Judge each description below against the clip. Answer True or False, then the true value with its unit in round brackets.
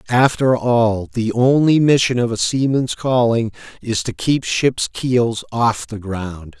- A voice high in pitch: False (120 Hz)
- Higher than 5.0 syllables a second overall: False (3.7 syllables/s)